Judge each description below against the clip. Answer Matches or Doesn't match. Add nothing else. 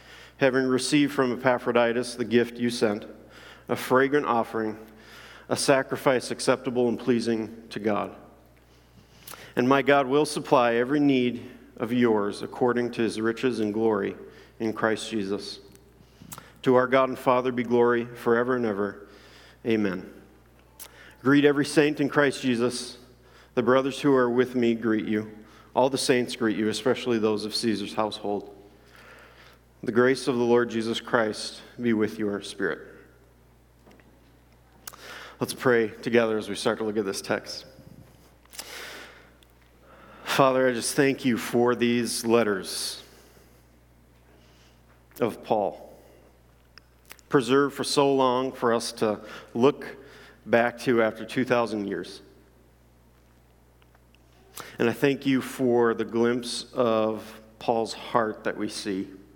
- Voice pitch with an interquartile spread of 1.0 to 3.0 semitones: Doesn't match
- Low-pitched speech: Matches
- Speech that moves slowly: Matches